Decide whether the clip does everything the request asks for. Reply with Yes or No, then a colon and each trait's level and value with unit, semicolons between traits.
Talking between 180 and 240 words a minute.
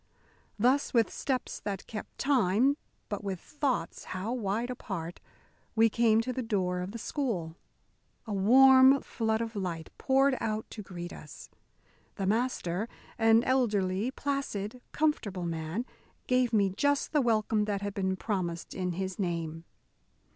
No: average, 145 wpm